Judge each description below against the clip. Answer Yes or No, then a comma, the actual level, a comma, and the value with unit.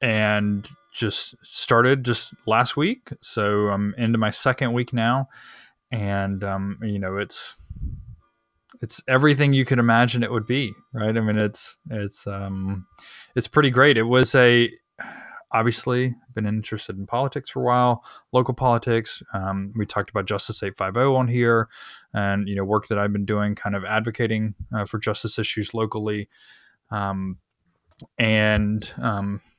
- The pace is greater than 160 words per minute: No, average, 150 wpm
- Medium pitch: No, low, 110 Hz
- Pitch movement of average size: Yes, average, 3.0 semitones